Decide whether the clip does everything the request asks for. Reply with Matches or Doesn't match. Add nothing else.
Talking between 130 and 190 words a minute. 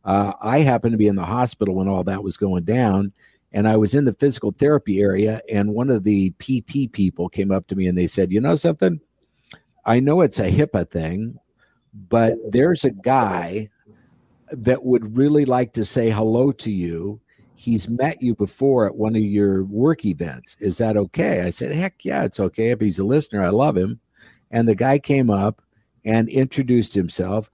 Doesn't match